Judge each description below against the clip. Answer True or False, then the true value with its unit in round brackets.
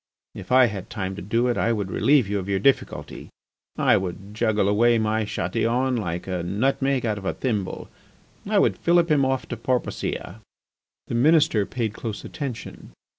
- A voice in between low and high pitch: False (110 Hz)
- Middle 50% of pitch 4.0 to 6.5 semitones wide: True (4.4 semitones)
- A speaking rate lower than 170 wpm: False (180 wpm)